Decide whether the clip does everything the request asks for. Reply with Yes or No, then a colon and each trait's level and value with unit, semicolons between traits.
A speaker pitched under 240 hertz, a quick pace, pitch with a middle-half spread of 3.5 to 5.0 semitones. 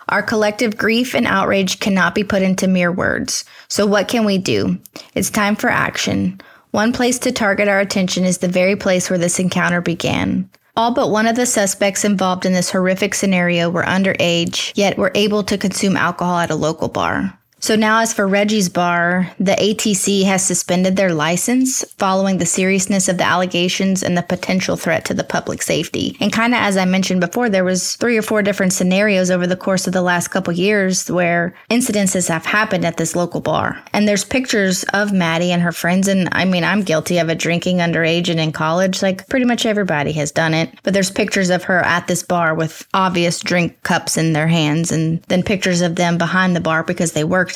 No: medium, 185 Hz; fast, 210 wpm; average, 2.8 semitones